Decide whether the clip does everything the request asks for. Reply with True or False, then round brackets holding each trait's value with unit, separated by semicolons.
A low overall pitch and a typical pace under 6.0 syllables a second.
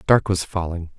True (90 Hz; 4.9 syllables/s)